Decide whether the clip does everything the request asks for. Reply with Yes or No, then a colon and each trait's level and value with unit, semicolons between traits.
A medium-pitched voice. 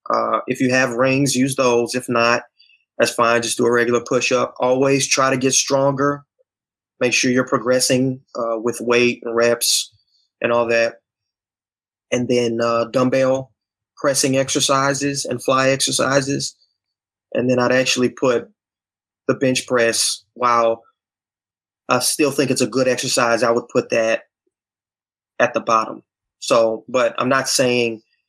No: low, 125 Hz